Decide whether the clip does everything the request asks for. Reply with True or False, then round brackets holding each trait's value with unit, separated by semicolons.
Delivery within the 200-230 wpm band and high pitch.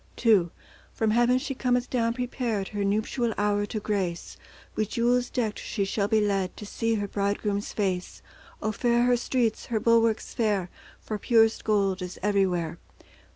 False (160 wpm; 215 Hz)